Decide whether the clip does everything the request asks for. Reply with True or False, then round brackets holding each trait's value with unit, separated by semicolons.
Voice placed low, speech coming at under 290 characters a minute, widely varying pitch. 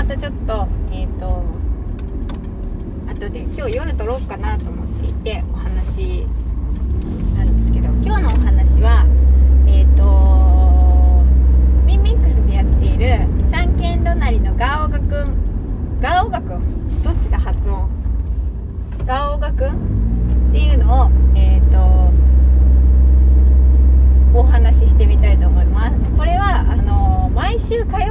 False (65 Hz; 235 characters per minute; 4.2 semitones)